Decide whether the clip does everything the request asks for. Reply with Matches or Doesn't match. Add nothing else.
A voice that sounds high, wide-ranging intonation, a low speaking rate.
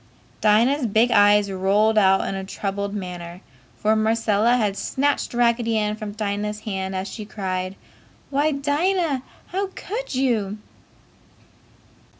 Doesn't match